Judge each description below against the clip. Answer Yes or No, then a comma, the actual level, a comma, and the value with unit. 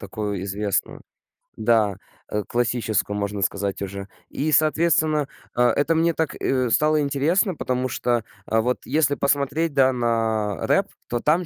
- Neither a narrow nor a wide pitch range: No, wide, 6.1 semitones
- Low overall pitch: Yes, low, 125 Hz